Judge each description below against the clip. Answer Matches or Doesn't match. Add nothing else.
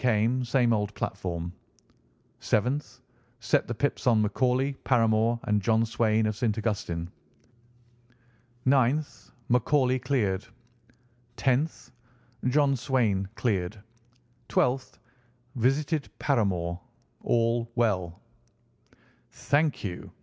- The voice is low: Matches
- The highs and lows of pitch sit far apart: Doesn't match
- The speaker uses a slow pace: Matches